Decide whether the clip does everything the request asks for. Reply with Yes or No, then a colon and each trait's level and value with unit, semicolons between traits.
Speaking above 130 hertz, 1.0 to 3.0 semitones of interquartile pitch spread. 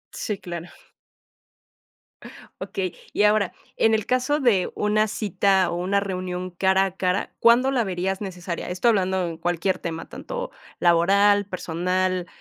Yes: high, 190 Hz; narrow, 2.6 semitones